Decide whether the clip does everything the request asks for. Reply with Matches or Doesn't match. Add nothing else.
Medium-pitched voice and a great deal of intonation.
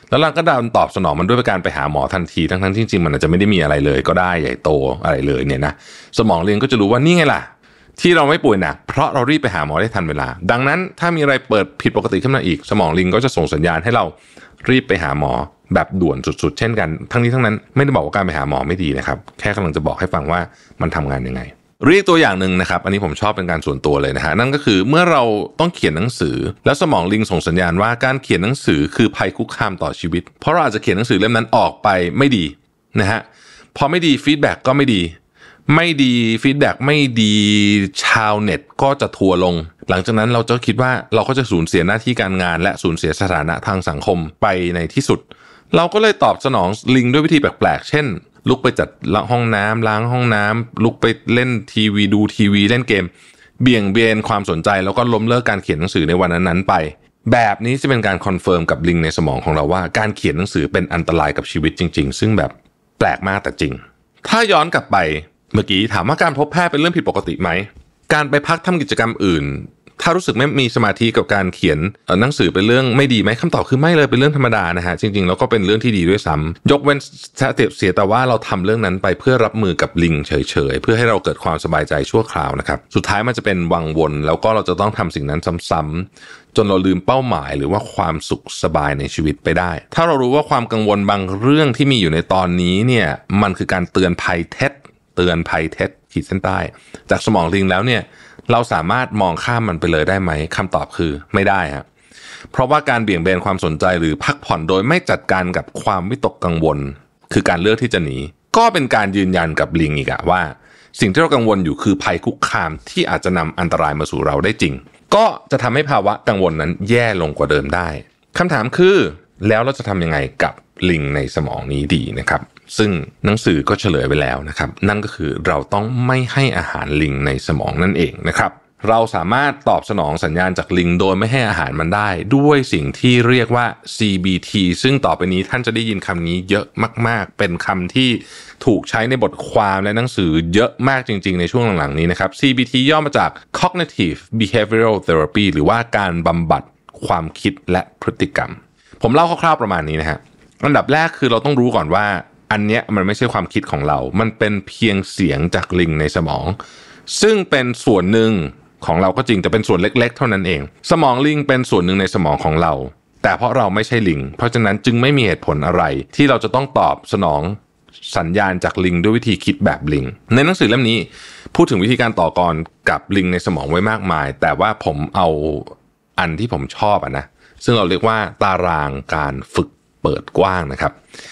Doesn't match